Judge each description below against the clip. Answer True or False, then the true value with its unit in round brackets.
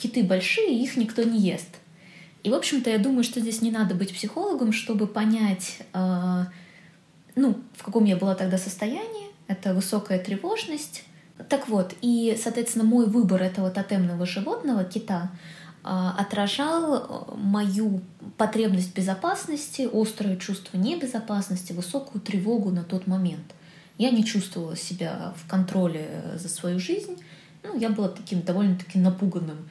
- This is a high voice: True (200 Hz)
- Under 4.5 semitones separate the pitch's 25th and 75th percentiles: True (4.1 semitones)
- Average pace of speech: True (135 wpm)